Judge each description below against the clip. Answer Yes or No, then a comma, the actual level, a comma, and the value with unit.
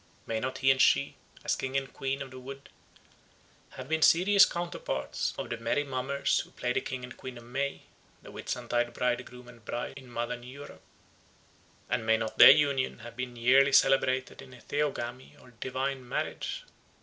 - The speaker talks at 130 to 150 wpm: No, average, 180 wpm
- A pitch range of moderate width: No, narrow, 2.0 semitones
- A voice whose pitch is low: Yes, low, 130 Hz